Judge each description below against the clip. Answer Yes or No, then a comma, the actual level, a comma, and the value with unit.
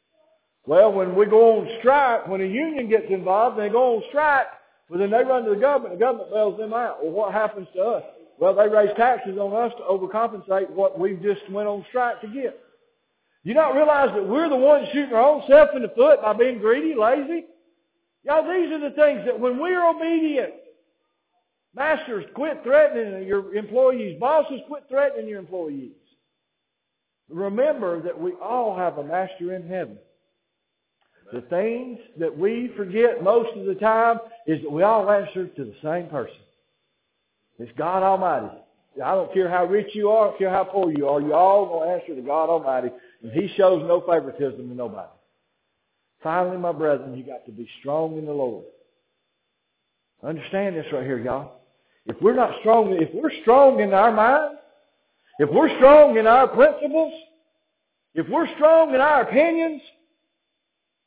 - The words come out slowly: No, average, 180 wpm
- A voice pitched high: Yes, high, 225 Hz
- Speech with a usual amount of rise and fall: No, wide, 7.6 semitones